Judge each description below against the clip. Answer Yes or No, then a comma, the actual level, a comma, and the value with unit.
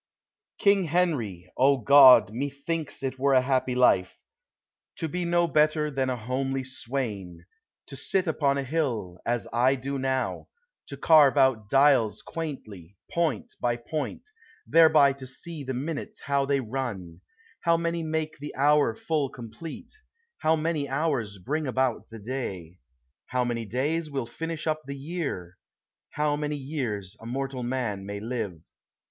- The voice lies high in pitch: No, low, 135 Hz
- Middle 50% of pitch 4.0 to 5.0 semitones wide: Yes, average, 4.4 semitones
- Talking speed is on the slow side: No, average, 155 wpm